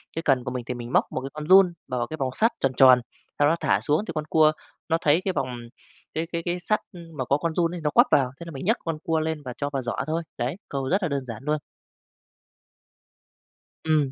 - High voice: No, medium, 150 Hz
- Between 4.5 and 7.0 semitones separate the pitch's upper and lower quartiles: No, average, 3.9 semitones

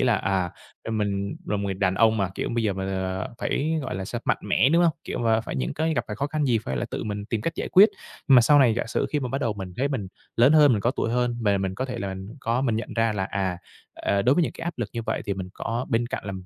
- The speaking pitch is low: Yes, low, 115 Hz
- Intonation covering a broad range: No, average, 4.5 semitones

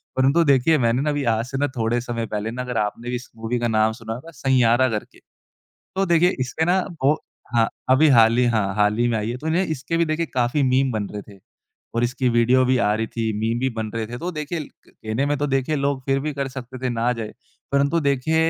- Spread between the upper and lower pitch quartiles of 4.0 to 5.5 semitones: No, average, 3.6 semitones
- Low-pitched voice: Yes, low, 125 Hz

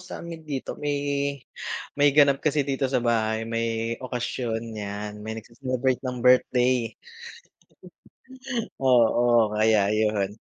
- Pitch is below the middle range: Yes, low, 120 Hz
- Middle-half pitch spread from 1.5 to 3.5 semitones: Yes, average, 3.0 semitones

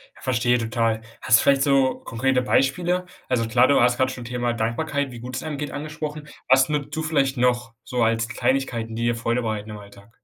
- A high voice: No, low, 125 Hz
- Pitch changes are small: No, average, 3.1 semitones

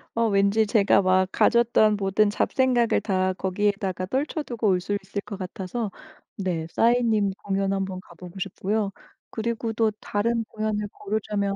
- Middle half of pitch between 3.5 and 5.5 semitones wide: No, narrow, 2.6 semitones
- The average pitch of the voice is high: Yes, high, 205 Hz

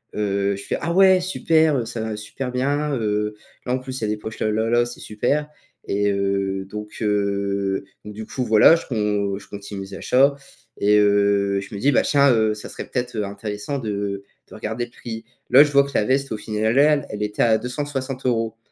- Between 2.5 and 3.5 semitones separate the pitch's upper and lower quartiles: No, average, 4.2 semitones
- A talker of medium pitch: No, low, 110 Hz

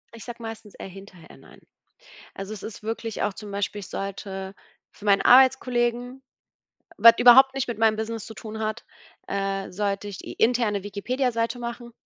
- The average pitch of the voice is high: Yes, high, 220 Hz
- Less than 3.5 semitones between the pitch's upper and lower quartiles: Yes, average, 3.1 semitones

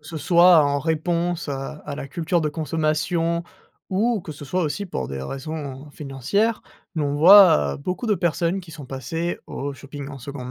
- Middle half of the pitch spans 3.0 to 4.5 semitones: Yes, average, 3.5 semitones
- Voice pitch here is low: No, medium, 155 Hz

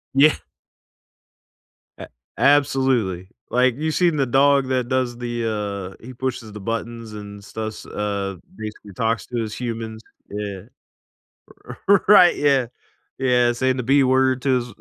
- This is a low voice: Yes, low, 120 Hz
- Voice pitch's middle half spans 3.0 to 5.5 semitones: Yes, average, 3.5 semitones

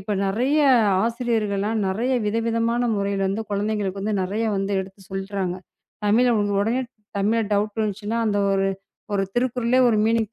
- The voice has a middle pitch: No, high, 210 Hz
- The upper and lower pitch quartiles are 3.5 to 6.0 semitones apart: No, narrow, 2.5 semitones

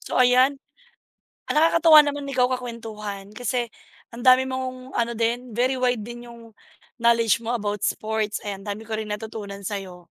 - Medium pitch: No, high, 235 Hz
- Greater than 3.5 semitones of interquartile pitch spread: No, average, 3.0 semitones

